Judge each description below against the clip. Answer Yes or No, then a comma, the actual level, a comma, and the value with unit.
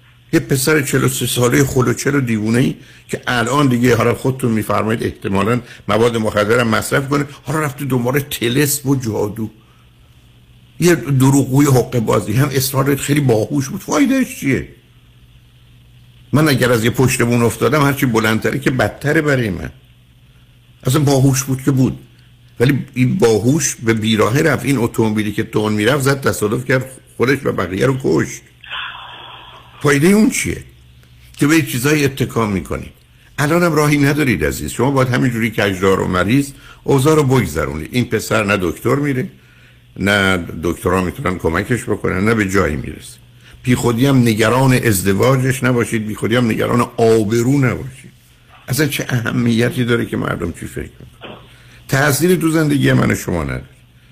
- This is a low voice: Yes, low, 125 Hz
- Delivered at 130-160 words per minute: Yes, average, 150 wpm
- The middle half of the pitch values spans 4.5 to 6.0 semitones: No, average, 3.8 semitones